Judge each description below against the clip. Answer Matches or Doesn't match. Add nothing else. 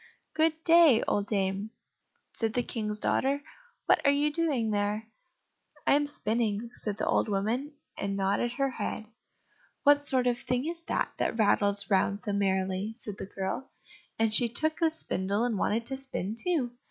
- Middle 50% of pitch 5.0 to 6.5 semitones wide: Matches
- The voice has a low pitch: Doesn't match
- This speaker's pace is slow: Doesn't match